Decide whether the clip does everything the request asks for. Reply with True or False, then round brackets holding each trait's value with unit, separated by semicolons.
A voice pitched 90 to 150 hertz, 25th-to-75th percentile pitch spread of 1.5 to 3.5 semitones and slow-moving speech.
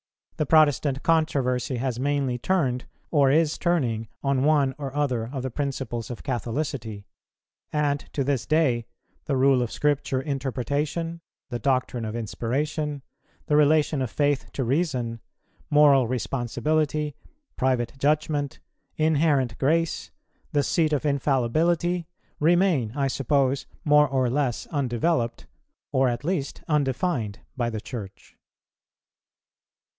True (140 Hz; 3.2 semitones; 120 wpm)